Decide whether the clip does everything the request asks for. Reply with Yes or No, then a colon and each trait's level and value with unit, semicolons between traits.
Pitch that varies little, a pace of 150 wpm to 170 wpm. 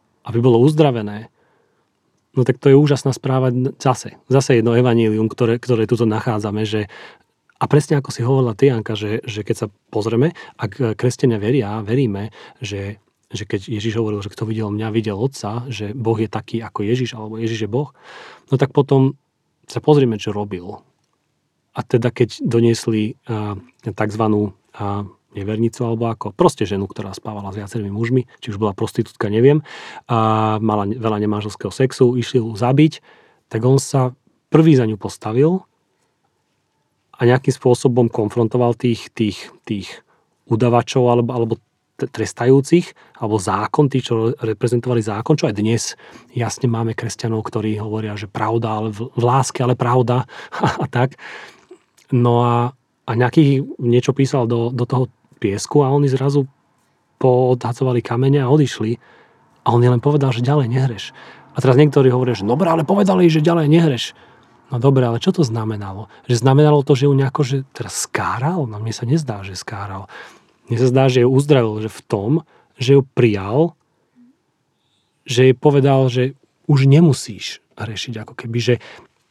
No: average, 3.4 semitones; average, 160 wpm